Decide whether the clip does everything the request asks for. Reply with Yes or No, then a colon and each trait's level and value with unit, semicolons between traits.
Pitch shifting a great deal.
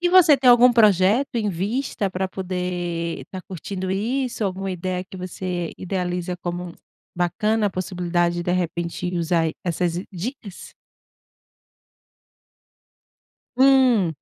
No: average, 3.4 semitones